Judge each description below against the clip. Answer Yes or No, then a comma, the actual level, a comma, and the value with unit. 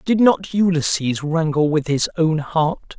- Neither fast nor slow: Yes, average, 160 wpm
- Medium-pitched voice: Yes, medium, 160 Hz